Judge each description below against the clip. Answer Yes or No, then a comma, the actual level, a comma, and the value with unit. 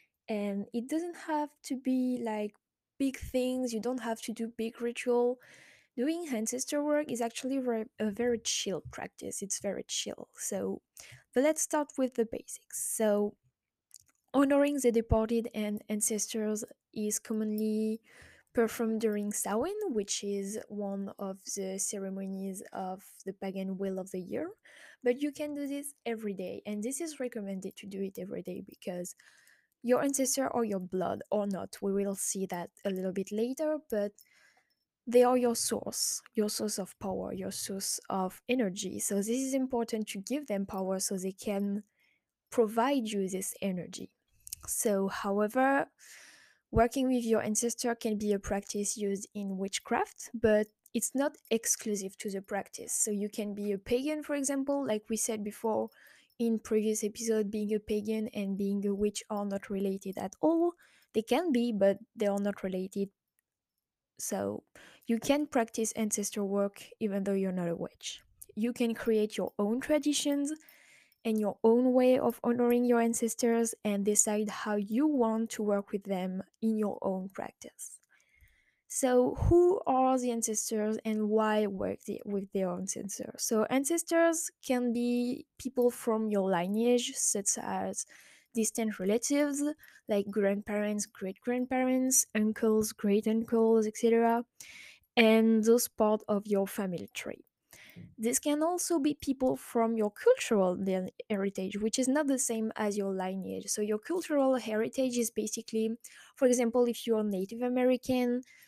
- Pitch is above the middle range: Yes, high, 220 Hz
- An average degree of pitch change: Yes, average, 3.5 semitones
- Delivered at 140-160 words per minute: Yes, average, 155 wpm